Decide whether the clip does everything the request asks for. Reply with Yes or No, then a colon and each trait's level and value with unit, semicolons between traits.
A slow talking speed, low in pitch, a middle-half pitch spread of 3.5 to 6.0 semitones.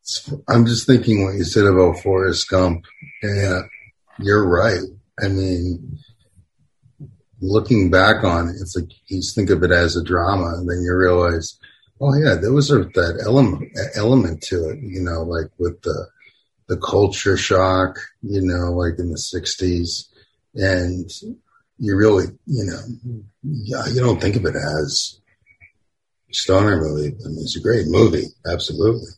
No: average, 155 wpm; very low, 95 Hz; average, 4.3 semitones